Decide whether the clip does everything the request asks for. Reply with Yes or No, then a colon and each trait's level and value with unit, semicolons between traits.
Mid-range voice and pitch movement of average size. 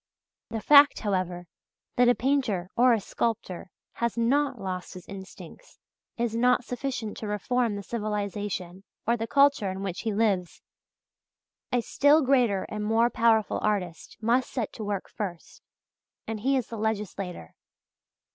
No: high, 220 Hz; average, 3.7 semitones